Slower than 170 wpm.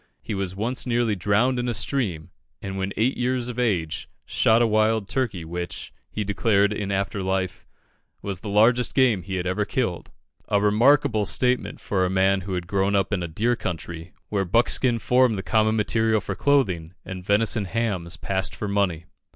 No: average, 190 wpm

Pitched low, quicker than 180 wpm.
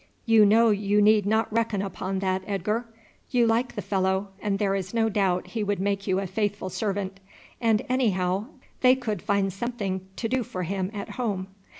No: high, 205 Hz; average, 190 wpm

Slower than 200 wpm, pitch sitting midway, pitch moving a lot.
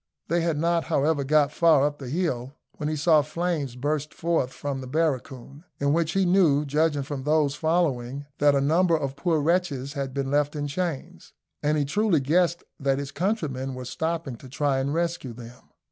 No: average, 190 wpm; medium, 145 Hz; average, 3.2 semitones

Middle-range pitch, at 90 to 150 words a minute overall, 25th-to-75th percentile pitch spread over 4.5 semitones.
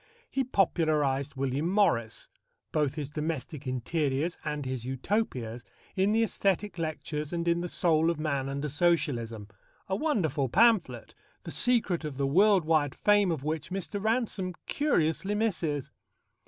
Yes: medium, 160 Hz; average, 140 wpm; wide, 5.6 semitones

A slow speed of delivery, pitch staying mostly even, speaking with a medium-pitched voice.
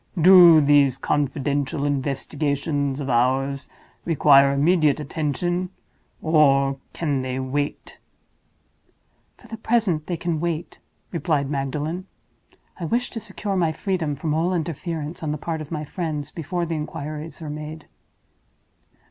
No: slow, 125 wpm; average, 3.1 semitones; medium, 150 Hz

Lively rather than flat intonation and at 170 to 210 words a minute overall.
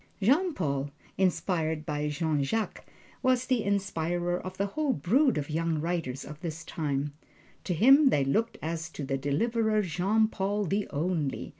No: wide, 5.9 semitones; average, 160 wpm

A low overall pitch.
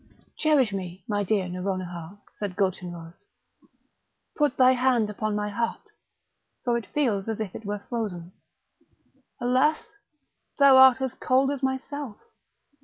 No: high, 220 Hz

